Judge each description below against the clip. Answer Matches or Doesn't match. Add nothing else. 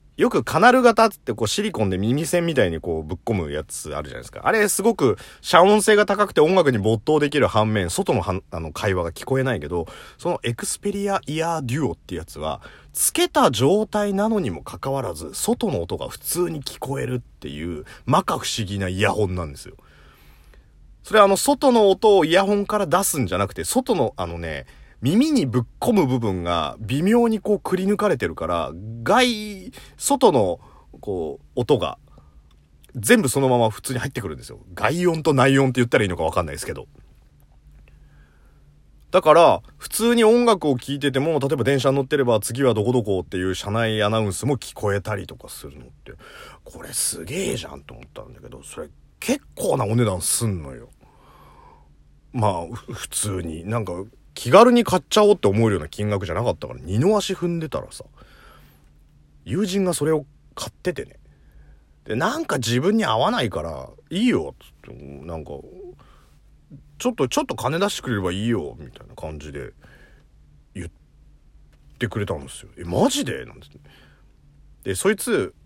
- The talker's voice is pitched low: Matches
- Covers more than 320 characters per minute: Matches